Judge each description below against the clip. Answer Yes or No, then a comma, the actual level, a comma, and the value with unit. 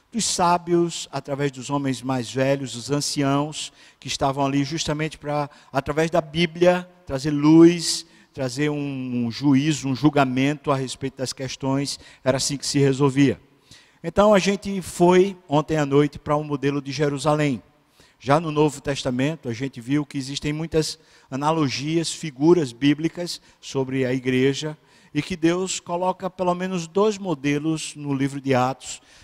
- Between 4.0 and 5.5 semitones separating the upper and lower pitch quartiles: No, average, 3.2 semitones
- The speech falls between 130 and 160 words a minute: Yes, average, 155 wpm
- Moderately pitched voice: Yes, medium, 145 Hz